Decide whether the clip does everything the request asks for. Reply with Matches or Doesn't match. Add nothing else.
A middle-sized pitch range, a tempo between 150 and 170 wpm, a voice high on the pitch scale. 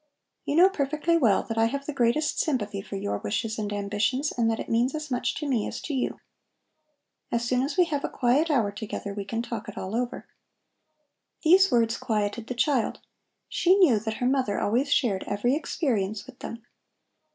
Doesn't match